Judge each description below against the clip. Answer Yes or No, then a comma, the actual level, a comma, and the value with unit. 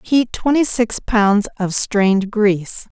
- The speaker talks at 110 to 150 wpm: Yes, average, 140 wpm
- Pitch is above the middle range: Yes, high, 215 Hz